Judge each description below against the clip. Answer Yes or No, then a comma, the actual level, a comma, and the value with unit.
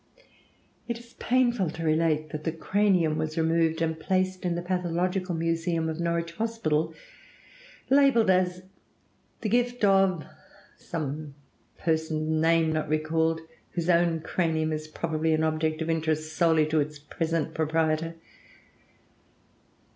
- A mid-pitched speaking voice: Yes, medium, 165 Hz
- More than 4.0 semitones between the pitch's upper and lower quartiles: No, narrow, 2.4 semitones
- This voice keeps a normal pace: No, slow, 130 wpm